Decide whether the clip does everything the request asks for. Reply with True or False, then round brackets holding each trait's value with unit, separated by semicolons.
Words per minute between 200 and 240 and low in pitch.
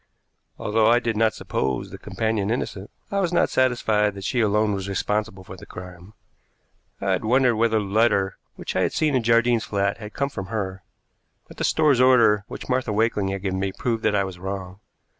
True (205 wpm; 105 Hz)